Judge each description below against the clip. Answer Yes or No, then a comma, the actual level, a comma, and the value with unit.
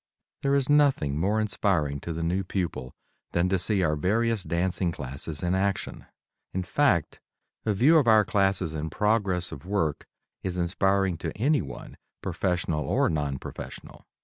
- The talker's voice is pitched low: Yes, very low, 95 Hz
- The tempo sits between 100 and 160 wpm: Yes, average, 155 wpm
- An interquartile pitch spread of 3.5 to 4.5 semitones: Yes, average, 4.2 semitones